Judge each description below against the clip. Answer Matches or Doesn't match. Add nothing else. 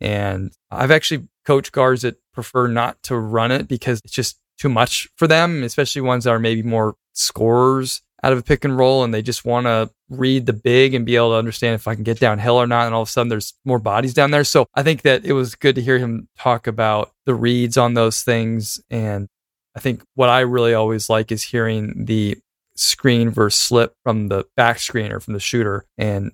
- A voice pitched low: Matches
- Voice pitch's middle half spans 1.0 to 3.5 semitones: Matches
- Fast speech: Matches